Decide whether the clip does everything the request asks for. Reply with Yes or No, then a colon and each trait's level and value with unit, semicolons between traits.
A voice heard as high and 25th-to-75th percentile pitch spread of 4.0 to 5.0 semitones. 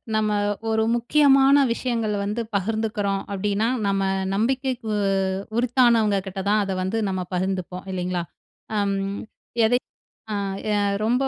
No: high, 215 Hz; average, 3.3 semitones